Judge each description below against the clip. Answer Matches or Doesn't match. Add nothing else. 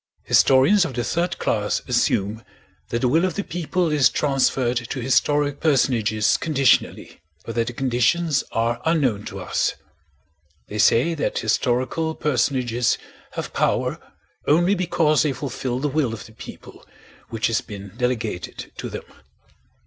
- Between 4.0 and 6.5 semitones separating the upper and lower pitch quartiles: Matches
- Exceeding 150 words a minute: Doesn't match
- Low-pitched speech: Matches